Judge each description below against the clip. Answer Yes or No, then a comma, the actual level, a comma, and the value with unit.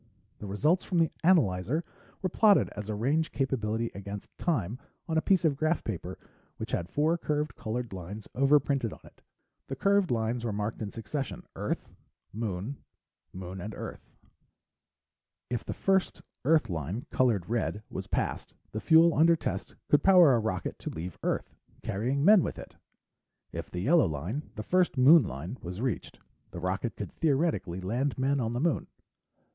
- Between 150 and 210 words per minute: Yes, average, 165 wpm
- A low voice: Yes, low, 120 Hz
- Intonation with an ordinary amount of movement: No, wide, 7.3 semitones